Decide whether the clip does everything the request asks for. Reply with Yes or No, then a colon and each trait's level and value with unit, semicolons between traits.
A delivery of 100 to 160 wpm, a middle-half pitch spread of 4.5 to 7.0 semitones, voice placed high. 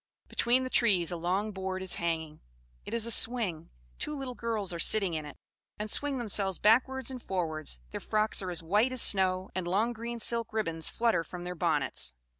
No: average, 200 wpm; average, 5.2 semitones; high, 195 Hz